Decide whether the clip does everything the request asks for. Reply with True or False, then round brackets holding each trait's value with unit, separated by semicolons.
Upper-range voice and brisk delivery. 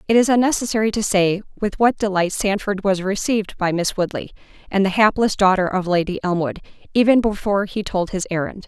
False (200 Hz; 185 wpm)